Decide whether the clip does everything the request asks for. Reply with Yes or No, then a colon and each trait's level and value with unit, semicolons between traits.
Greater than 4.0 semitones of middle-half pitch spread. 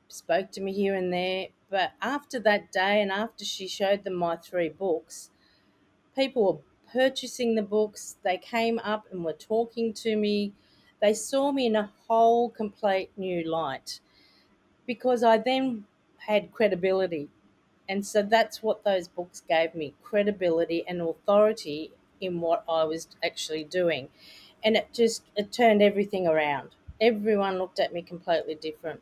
Yes: average, 4.6 semitones